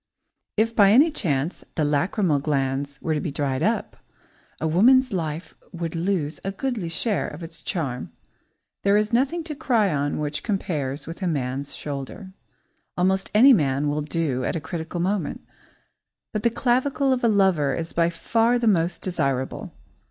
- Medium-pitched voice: Yes, medium, 170 Hz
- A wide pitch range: Yes, wide, 6.4 semitones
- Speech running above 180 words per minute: No, average, 165 wpm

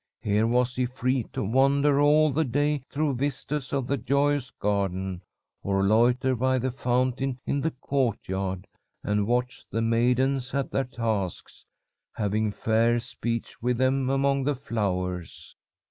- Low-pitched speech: Yes, low, 125 Hz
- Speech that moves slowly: No, average, 145 wpm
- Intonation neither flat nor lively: Yes, average, 3.7 semitones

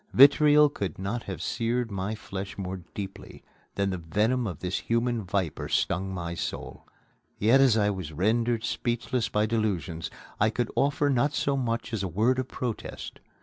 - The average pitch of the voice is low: Yes, low, 110 Hz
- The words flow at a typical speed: Yes, average, 170 wpm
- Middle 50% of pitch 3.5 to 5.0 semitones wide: Yes, average, 4.2 semitones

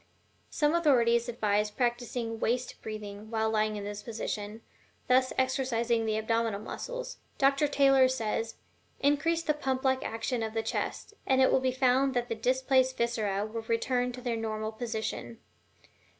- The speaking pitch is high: Yes, high, 235 Hz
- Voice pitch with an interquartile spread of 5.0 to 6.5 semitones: No, average, 3.0 semitones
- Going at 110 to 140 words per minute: No, average, 155 wpm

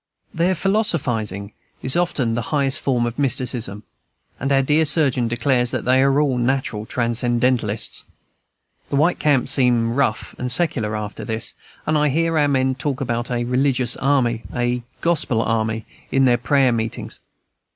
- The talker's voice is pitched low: Yes, low, 125 Hz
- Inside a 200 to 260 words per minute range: No, average, 155 wpm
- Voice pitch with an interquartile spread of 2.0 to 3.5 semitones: Yes, average, 3.2 semitones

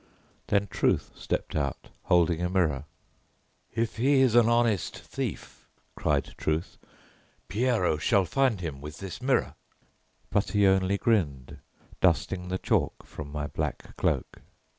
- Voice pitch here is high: No, very low, 95 Hz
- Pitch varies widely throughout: Yes, wide, 6.2 semitones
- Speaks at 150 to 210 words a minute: No, slow, 135 wpm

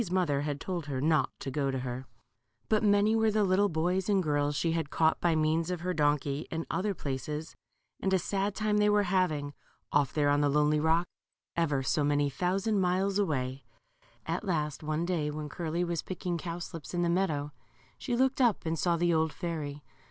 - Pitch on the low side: No, medium, 165 Hz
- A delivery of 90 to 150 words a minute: No, average, 180 wpm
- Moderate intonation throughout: Yes, average, 4.1 semitones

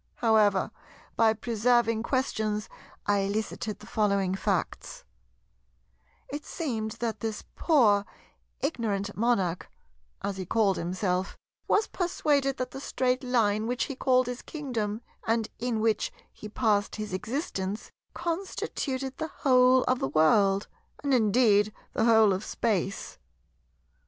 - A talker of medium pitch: No, high, 220 Hz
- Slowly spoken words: Yes, slow, 120 wpm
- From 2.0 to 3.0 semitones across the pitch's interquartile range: No, average, 3.8 semitones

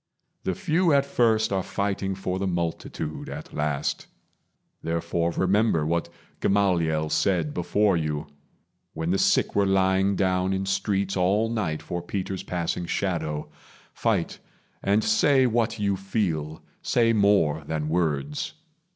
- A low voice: Yes, very low, 95 Hz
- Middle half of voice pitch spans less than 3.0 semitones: No, average, 3.6 semitones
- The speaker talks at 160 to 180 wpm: No, slow, 135 wpm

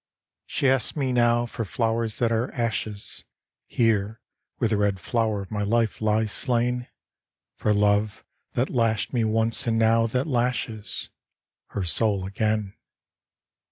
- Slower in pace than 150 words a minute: Yes, average, 140 wpm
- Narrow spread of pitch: Yes, narrow, 2.0 semitones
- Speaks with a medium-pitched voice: No, low, 115 Hz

